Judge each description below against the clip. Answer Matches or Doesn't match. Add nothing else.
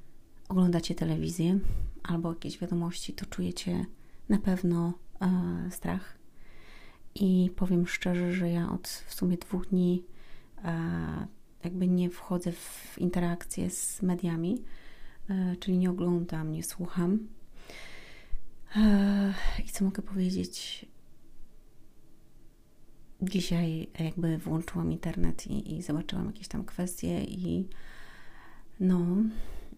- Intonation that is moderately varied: Doesn't match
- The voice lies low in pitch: Doesn't match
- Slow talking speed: Matches